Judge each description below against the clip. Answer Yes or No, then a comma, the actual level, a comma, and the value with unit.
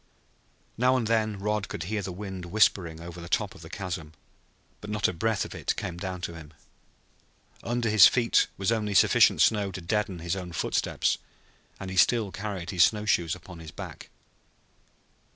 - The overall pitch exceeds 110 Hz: No, very low, 95 Hz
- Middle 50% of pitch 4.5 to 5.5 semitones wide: No, average, 3.6 semitones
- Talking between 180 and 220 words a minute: Yes, average, 185 wpm